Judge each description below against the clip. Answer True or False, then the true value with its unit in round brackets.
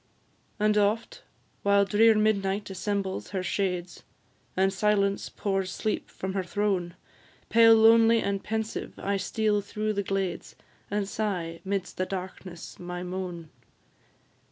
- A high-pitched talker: True (200 Hz)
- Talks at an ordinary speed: False (130 wpm)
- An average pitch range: False (2.1 semitones)